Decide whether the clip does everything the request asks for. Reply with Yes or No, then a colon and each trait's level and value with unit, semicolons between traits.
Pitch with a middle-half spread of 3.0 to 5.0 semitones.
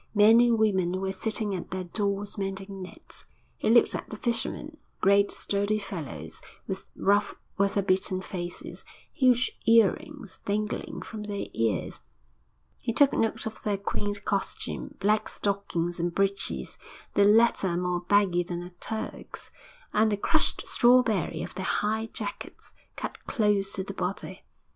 No: narrow, 2.5 semitones